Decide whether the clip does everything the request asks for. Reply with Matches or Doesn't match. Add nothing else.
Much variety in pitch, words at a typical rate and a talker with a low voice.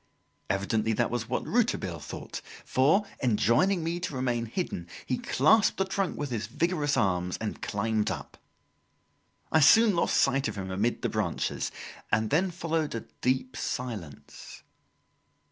Matches